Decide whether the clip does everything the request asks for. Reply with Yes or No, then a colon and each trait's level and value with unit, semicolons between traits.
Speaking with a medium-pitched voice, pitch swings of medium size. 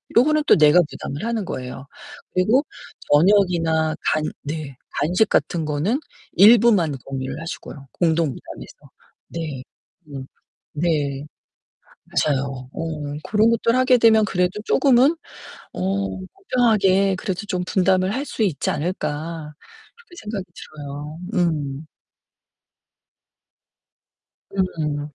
No: medium, 175 Hz; wide, 6.0 semitones